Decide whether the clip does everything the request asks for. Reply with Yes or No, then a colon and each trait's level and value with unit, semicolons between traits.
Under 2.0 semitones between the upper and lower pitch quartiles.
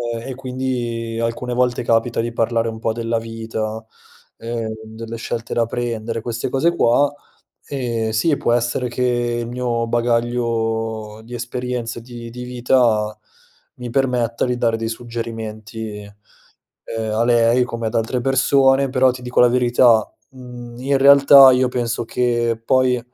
Yes: narrow, 1.6 semitones